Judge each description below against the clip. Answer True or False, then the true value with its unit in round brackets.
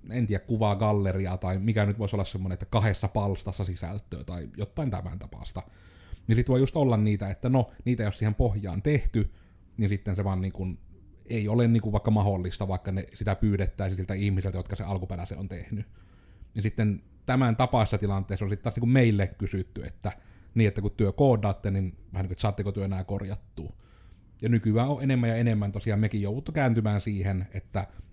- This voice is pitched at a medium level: False (100 Hz)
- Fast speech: True (185 wpm)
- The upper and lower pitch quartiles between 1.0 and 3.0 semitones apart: True (2.4 semitones)